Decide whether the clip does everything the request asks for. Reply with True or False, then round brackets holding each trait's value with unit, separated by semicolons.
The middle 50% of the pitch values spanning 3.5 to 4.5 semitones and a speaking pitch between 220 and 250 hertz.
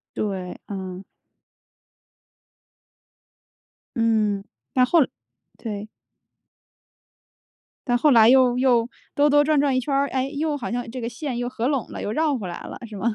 True (4.2 semitones; 245 Hz)